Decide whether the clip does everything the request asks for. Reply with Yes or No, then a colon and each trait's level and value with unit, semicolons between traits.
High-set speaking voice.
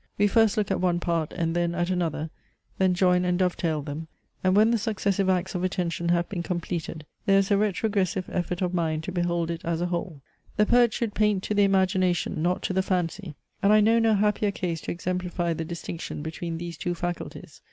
No: medium, 180 Hz